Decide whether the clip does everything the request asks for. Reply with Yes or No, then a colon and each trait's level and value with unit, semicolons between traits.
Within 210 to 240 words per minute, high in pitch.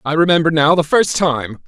No: fast, 215 wpm; medium, 155 Hz